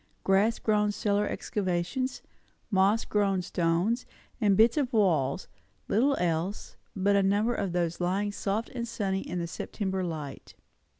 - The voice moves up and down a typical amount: Yes, average, 3.2 semitones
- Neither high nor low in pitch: No, high, 200 Hz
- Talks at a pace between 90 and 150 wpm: Yes, average, 140 wpm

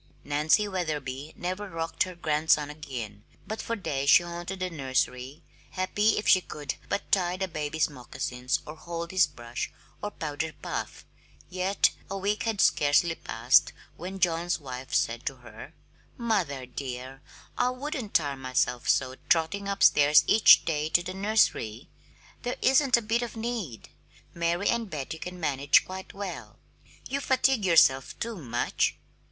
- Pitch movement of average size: No, wide, 6.1 semitones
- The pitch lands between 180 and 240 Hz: No, medium, 165 Hz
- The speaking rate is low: No, average, 150 wpm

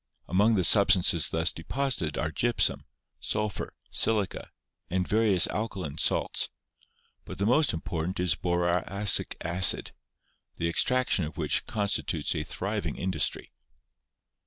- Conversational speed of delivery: No, slow, 115 wpm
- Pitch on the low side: Yes, very low, 95 Hz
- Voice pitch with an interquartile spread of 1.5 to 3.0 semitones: No, average, 4.1 semitones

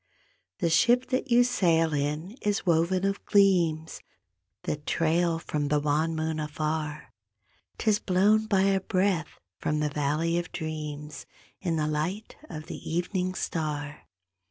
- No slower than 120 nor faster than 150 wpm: Yes, average, 140 wpm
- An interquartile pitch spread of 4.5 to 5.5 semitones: No, average, 3.9 semitones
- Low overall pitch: No, medium, 165 Hz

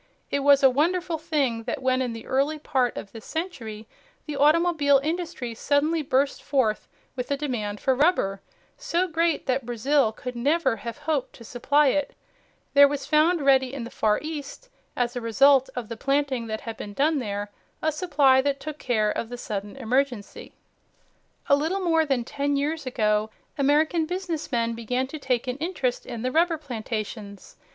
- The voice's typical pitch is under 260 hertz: No, very high, 275 Hz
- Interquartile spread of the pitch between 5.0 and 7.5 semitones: No, average, 4.3 semitones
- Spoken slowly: No, average, 180 wpm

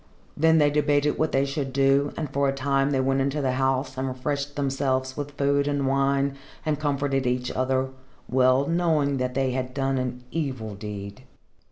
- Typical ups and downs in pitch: No, narrow, 1.6 semitones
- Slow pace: No, average, 185 wpm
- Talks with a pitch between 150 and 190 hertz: No, low, 135 Hz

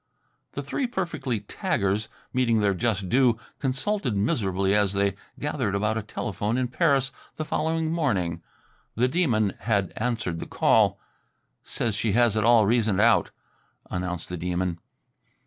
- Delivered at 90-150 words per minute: Yes, average, 145 wpm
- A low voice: Yes, low, 110 Hz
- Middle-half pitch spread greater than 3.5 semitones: Yes, average, 4.5 semitones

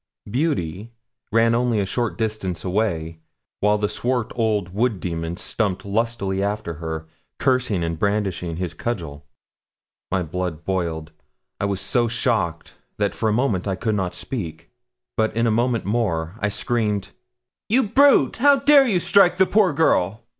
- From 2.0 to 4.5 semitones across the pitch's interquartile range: No, average, 5.0 semitones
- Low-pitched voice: Yes, low, 105 Hz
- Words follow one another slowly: No, average, 155 wpm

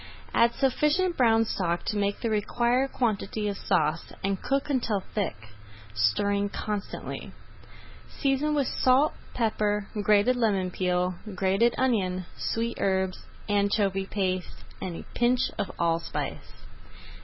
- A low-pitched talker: No, high, 205 Hz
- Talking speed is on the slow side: Yes, slow, 120 wpm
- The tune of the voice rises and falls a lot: No, average, 4.2 semitones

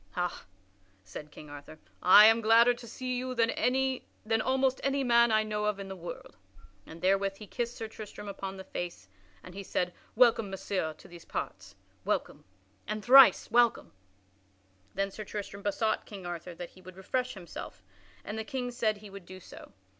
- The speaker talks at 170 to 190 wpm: Yes, average, 180 wpm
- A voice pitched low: No, high, 210 Hz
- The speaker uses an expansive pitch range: No, average, 4.2 semitones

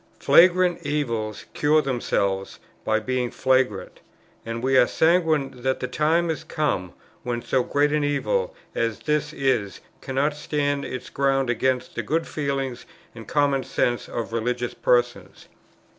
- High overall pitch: No, low, 135 Hz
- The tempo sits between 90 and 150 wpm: Yes, average, 145 wpm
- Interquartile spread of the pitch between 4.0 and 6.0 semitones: No, average, 3.6 semitones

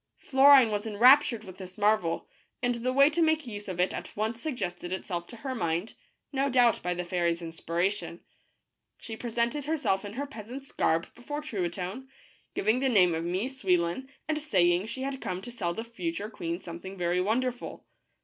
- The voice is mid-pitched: No, high, 215 Hz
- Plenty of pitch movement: Yes, wide, 6.4 semitones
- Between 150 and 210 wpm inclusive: Yes, average, 190 wpm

